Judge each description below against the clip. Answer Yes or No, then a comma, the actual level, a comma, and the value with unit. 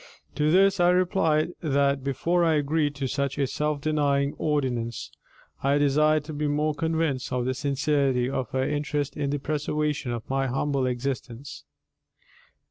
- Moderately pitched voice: Yes, medium, 145 Hz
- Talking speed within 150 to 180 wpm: Yes, average, 155 wpm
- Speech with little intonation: Yes, narrow, 2.1 semitones